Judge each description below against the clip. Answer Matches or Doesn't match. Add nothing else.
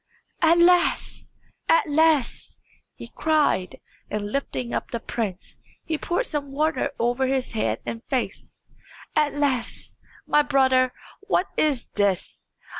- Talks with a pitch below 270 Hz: Doesn't match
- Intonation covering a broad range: Doesn't match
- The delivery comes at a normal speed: Doesn't match